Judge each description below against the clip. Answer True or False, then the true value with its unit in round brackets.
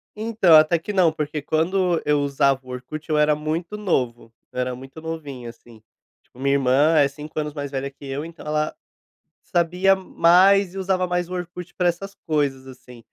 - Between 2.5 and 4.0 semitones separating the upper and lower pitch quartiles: False (4.4 semitones)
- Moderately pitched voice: True (155 Hz)